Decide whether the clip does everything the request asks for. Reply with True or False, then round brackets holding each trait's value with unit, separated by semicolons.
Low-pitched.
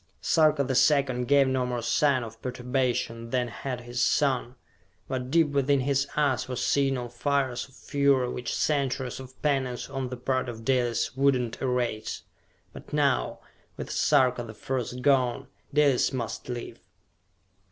True (130 Hz)